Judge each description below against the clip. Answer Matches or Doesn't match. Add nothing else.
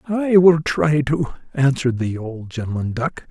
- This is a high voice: Doesn't match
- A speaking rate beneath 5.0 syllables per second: Matches